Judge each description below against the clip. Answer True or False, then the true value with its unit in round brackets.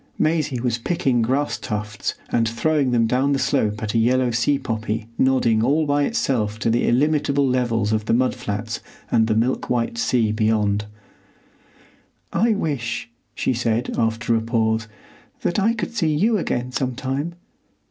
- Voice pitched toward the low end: True (120 Hz)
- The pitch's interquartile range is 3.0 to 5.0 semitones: True (3.9 semitones)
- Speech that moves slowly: False (160 wpm)